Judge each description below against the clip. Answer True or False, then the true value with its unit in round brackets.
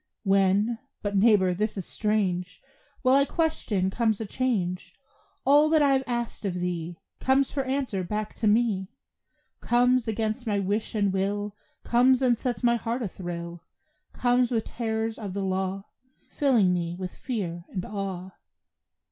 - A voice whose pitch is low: False (210 Hz)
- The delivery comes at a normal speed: True (155 wpm)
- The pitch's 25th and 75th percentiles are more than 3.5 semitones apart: True (4.2 semitones)